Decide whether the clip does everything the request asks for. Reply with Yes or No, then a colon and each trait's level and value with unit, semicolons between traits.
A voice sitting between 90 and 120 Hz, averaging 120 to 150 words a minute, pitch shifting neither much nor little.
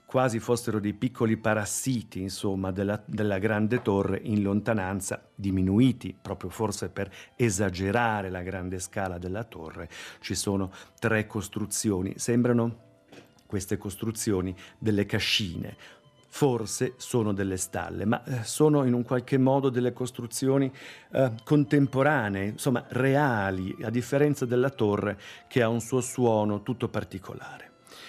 Yes: low, 110 Hz; average, 125 wpm; average, 4.0 semitones